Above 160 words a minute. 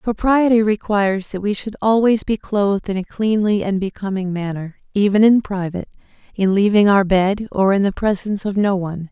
Yes: average, 185 wpm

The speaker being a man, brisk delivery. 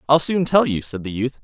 Yes: male; fast, 295 wpm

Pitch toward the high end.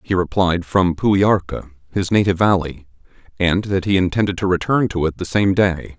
No: very low, 95 Hz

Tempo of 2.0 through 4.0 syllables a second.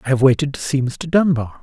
No: 6.0 syllables/s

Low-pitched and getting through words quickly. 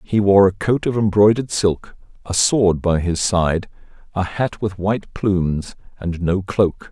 No: very low, 95 Hz; average, 175 wpm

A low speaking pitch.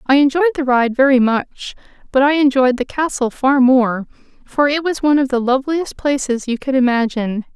No: very high, 265 Hz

